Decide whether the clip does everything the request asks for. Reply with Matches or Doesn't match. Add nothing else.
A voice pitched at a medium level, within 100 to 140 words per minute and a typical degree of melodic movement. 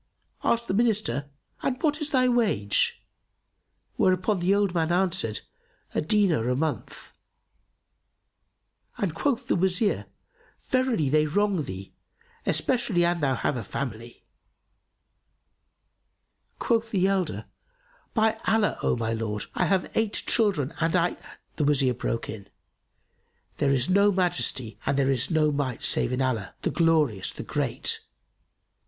Doesn't match